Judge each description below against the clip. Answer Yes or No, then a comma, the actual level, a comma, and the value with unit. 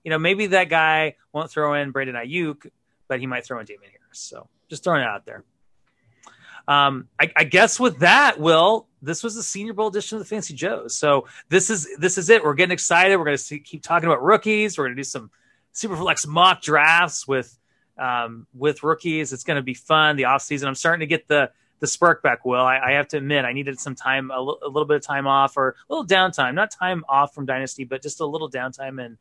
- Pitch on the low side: No, medium, 150 Hz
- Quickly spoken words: Yes, fast, 240 wpm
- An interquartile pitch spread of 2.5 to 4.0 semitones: No, average, 4.7 semitones